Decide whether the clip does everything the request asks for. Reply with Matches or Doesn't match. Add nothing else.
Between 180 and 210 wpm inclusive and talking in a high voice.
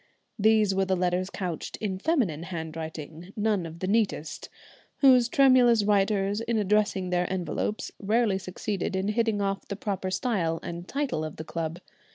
Doesn't match